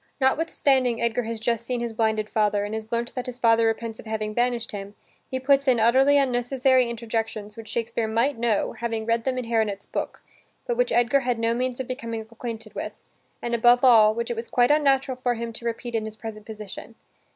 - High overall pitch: Yes, high, 235 Hz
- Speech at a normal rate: No, fast, 210 wpm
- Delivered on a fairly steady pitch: Yes, narrow, 2.1 semitones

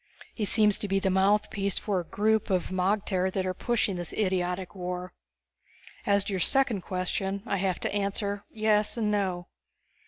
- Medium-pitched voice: No, high, 195 Hz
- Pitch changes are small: Yes, narrow, 2.2 semitones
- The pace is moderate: Yes, average, 175 wpm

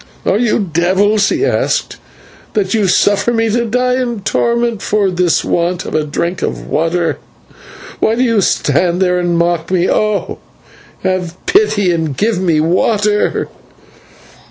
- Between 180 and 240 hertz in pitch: Yes, high, 190 Hz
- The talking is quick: No, average, 150 wpm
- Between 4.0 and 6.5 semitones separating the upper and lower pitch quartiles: Yes, average, 4.4 semitones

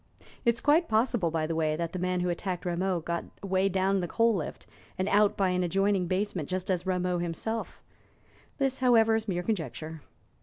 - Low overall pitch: No, medium, 185 Hz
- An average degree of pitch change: Yes, average, 3.5 semitones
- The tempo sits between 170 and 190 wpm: No, average, 200 wpm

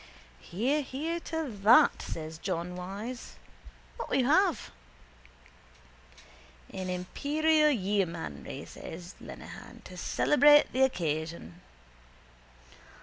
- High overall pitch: Yes, high, 210 Hz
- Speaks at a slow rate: Yes, slow, 90 wpm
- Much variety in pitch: Yes, wide, 9.0 semitones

